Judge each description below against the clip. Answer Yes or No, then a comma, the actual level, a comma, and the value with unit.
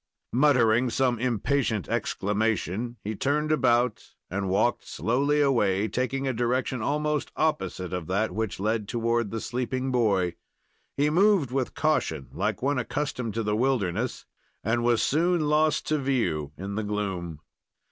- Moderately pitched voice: No, low, 120 Hz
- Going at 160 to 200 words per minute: No, average, 145 wpm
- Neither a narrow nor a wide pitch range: Yes, average, 4.7 semitones